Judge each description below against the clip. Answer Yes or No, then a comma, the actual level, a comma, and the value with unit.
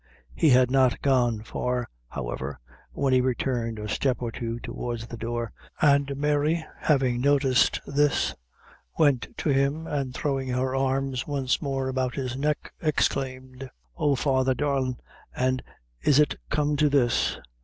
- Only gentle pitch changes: Yes, narrow, 2.3 semitones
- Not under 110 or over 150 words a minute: Yes, average, 145 wpm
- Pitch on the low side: Yes, low, 130 Hz